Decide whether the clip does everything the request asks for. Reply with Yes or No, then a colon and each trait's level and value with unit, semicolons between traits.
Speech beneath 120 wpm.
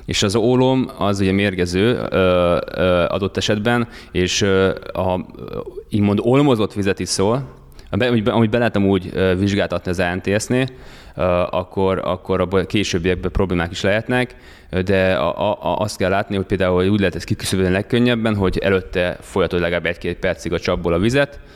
No: fast, 155 wpm